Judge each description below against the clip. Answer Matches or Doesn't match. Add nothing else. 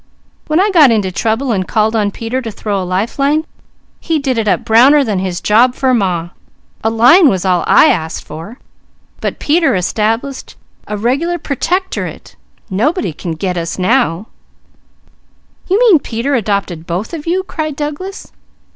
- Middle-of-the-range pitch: Doesn't match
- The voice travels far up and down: Matches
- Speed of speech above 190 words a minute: Doesn't match